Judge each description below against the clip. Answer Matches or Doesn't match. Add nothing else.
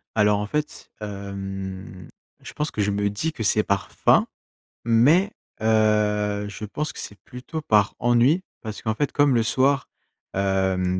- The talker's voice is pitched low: Matches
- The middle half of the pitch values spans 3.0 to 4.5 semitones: Matches